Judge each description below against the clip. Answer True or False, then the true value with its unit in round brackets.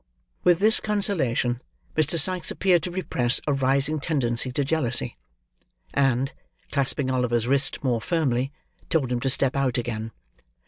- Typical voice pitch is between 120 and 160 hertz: True (135 Hz)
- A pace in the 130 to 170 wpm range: True (140 wpm)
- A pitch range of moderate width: True (4.4 semitones)